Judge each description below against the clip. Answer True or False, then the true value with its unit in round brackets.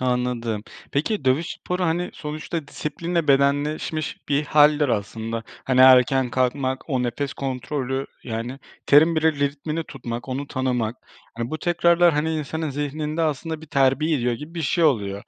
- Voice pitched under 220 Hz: True (140 Hz)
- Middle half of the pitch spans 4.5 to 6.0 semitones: False (3.6 semitones)